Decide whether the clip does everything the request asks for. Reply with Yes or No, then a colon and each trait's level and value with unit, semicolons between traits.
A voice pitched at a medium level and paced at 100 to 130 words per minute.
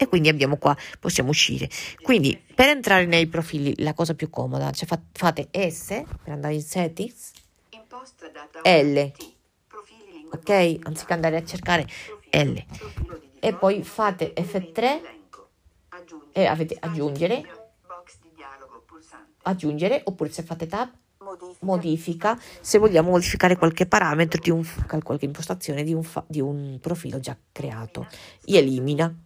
Yes: medium, 165 Hz; average, 125 wpm